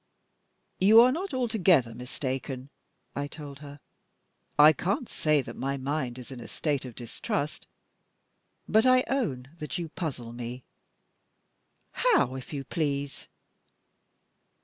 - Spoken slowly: Yes, slow, 125 wpm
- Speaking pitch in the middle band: Yes, medium, 145 Hz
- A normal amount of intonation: No, wide, 6.0 semitones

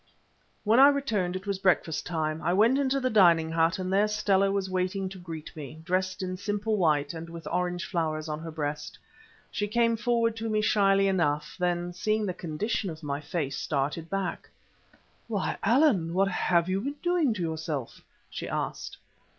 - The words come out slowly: No, average, 185 wpm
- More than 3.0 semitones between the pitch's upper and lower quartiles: Yes, average, 4.4 semitones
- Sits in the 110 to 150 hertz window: No, medium, 185 Hz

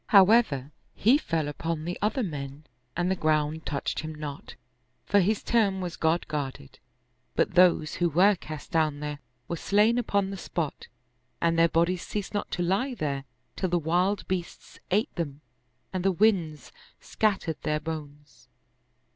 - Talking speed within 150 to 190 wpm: Yes, average, 160 wpm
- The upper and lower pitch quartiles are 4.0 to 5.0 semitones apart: Yes, average, 4.3 semitones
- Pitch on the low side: No, medium, 170 Hz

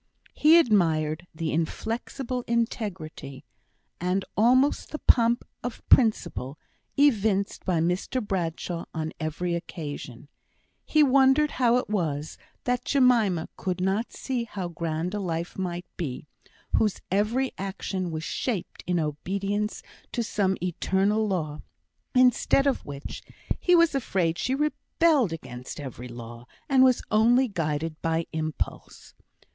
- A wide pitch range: Yes, wide, 6.9 semitones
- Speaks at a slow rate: Yes, slow, 125 wpm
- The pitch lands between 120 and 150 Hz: No, high, 190 Hz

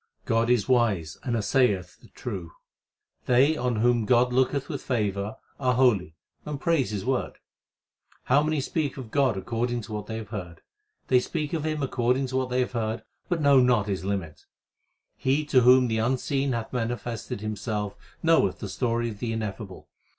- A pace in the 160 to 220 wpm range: Yes, average, 180 wpm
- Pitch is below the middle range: Yes, low, 120 Hz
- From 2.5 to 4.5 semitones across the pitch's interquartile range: Yes, average, 3.7 semitones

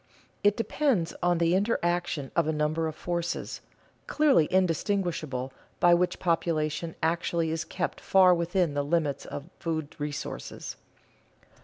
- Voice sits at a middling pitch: Yes, medium, 170 Hz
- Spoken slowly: Yes, slow, 130 wpm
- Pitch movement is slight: Yes, narrow, 2.3 semitones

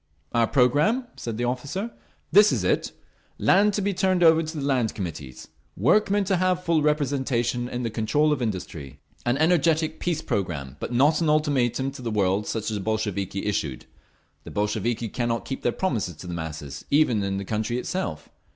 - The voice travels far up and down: Yes, wide, 7.2 semitones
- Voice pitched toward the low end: Yes, low, 125 Hz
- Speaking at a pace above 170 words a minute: Yes, average, 185 wpm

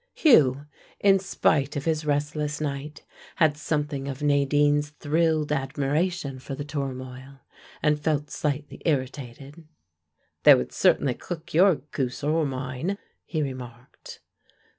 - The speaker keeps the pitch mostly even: Yes, narrow, 2.1 semitones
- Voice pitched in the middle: Yes, medium, 145 Hz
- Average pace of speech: No, slow, 120 wpm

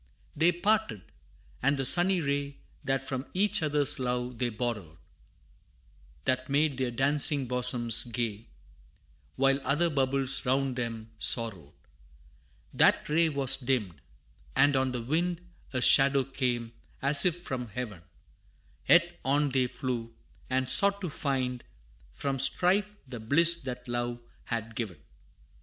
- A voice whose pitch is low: Yes, low, 130 Hz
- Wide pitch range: No, average, 3.2 semitones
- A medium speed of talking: No, slow, 130 wpm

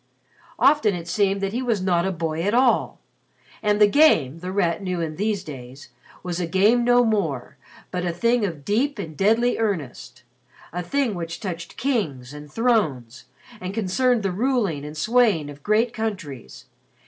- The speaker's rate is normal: Yes, average, 170 wpm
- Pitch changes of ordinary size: No, wide, 6.0 semitones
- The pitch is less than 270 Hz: Yes, high, 190 Hz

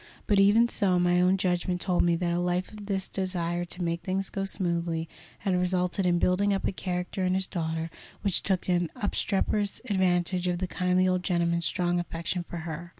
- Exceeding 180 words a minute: Yes, average, 200 wpm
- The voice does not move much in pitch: Yes, narrow, 1.6 semitones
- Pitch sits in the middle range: Yes, medium, 180 Hz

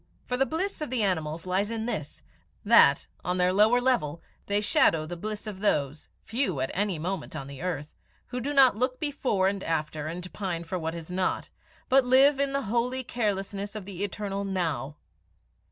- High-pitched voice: Yes, high, 195 Hz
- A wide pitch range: Yes, wide, 6.4 semitones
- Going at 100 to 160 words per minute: No, average, 190 wpm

